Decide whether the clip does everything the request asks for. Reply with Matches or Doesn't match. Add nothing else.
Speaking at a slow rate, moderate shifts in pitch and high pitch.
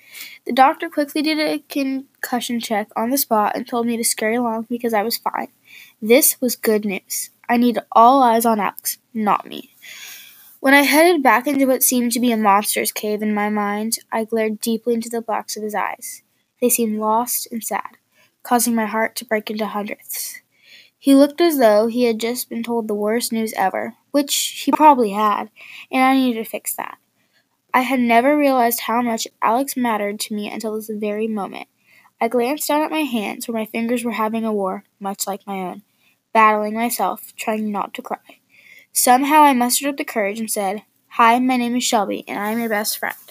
Doesn't match